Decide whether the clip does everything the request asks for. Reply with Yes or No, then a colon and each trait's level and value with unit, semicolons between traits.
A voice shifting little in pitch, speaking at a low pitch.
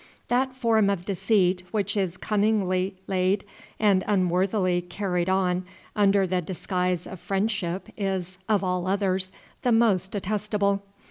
No: narrow, 2.1 semitones; high, 195 Hz